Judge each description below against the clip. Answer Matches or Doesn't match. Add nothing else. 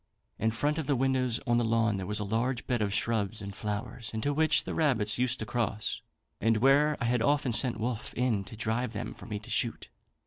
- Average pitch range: Matches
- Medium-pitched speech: Doesn't match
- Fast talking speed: Matches